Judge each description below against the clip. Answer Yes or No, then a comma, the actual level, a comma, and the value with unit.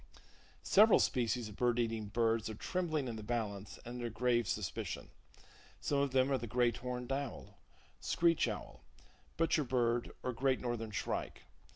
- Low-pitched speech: Yes, low, 120 Hz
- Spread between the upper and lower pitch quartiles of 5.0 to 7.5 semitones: No, average, 2.7 semitones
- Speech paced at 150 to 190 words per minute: Yes, average, 160 wpm